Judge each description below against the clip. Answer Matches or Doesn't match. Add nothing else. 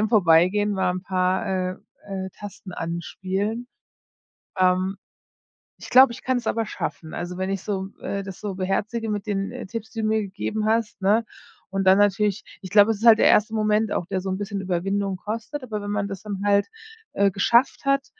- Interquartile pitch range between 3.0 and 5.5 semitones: Doesn't match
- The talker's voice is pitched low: Doesn't match